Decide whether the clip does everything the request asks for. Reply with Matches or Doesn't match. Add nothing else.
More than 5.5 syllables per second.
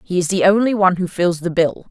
Matches